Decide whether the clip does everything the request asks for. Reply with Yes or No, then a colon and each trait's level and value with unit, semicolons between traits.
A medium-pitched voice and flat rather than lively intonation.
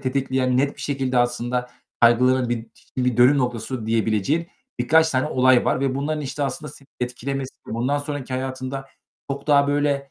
No: low, 130 Hz; narrow, 2.2 semitones